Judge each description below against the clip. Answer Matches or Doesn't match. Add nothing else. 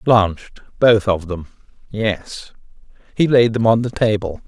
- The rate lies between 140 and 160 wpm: Matches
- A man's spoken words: Matches